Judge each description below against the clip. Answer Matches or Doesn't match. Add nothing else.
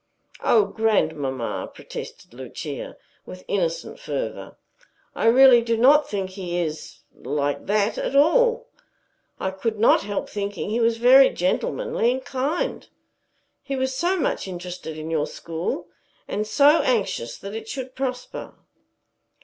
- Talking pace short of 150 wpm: Matches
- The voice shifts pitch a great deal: Matches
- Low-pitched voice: Doesn't match